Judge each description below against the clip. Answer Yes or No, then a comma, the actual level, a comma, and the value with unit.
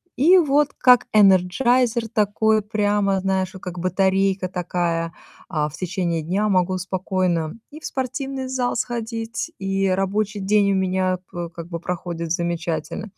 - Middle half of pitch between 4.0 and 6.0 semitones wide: No, average, 3.5 semitones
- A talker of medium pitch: No, high, 195 Hz